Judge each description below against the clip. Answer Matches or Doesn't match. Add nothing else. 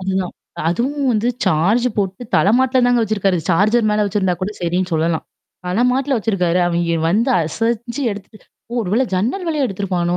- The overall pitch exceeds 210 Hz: Doesn't match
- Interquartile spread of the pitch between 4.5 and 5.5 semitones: Matches